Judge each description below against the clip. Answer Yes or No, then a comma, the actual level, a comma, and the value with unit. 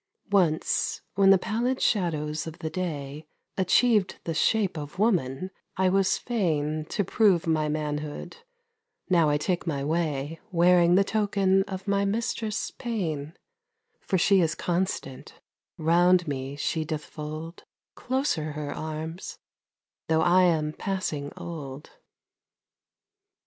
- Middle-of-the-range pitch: Yes, medium, 170 Hz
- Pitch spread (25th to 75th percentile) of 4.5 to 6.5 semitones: No, average, 4.1 semitones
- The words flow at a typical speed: No, slow, 125 wpm